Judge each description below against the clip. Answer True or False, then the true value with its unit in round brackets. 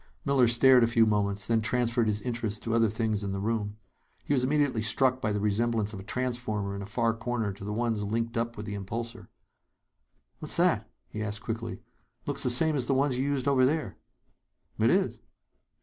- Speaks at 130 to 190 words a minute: False (205 wpm)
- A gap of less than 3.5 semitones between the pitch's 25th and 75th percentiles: True (2.9 semitones)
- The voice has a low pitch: True (115 Hz)